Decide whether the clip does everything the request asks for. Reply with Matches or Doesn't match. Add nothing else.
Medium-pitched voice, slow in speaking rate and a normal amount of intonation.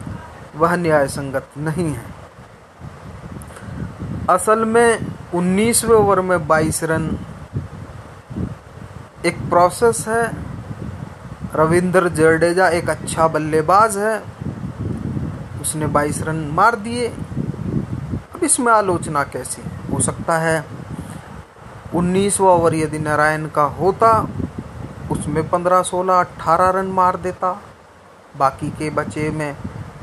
Matches